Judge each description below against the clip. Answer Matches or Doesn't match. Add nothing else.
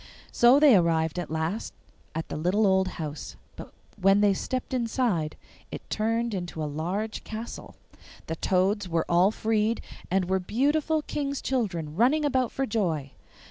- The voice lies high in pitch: Matches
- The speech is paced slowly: Doesn't match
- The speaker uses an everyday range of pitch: Doesn't match